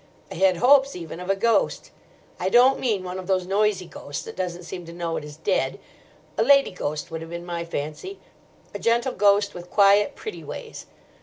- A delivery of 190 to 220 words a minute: Yes, fast, 205 wpm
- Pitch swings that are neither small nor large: Yes, average, 4.3 semitones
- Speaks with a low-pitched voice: No, medium, 185 Hz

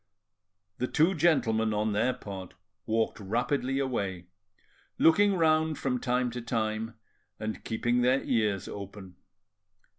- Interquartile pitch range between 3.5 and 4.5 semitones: Yes, average, 4.0 semitones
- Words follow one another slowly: Yes, slow, 120 wpm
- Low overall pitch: Yes, low, 115 Hz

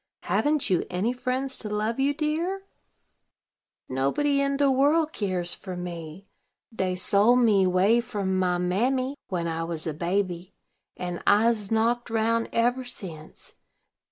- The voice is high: Yes, high, 210 Hz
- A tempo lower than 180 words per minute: Yes, average, 140 wpm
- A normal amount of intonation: No, wide, 6.0 semitones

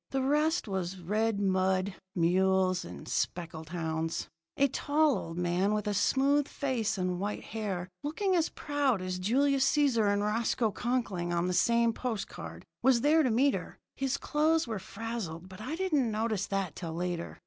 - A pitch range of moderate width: No, wide, 6.5 semitones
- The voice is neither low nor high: No, high, 215 Hz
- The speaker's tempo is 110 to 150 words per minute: No, average, 170 wpm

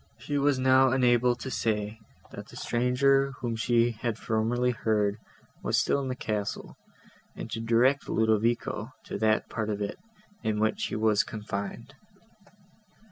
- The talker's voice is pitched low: Yes, low, 115 Hz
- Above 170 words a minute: No, average, 150 wpm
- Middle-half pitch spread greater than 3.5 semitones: No, narrow, 2.6 semitones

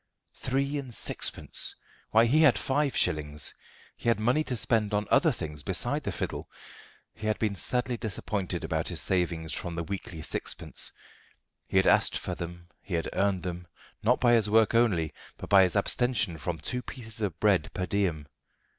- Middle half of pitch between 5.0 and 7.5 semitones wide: Yes, wide, 5.5 semitones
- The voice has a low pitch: Yes, low, 100 Hz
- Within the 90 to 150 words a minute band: No, average, 180 wpm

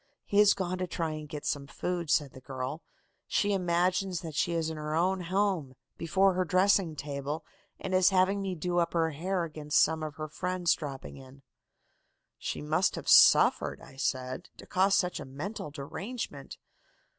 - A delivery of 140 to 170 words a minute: No, average, 180 wpm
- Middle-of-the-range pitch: Yes, medium, 170 Hz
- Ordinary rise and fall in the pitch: Yes, average, 3.8 semitones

